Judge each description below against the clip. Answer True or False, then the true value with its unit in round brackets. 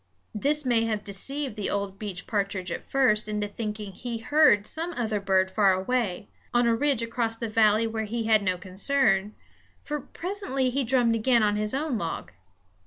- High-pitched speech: True (220 Hz)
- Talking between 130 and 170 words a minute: False (185 wpm)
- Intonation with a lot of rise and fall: False (3.8 semitones)